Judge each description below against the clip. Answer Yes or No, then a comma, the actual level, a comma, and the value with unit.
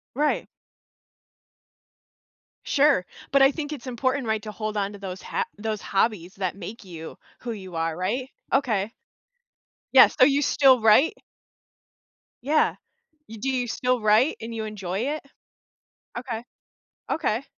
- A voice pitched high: Yes, high, 225 Hz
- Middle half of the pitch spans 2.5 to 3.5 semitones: No, average, 4.8 semitones